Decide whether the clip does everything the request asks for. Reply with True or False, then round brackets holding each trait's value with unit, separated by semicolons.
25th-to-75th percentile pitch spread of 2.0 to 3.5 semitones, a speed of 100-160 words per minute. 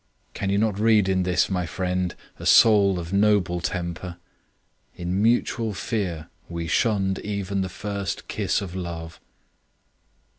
True (2.6 semitones; 140 wpm)